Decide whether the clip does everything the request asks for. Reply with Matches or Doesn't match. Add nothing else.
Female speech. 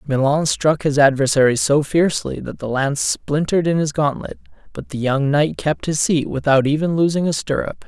Doesn't match